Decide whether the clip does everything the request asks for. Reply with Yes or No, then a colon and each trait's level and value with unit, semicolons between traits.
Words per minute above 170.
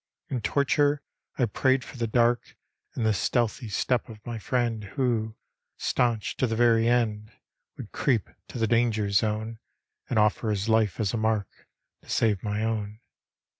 No: average, 165 wpm